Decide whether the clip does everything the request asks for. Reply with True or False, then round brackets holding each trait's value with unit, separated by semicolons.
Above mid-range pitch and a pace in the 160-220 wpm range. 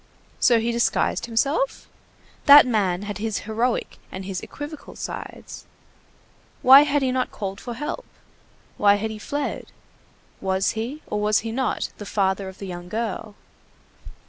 False (220 Hz; 150 wpm)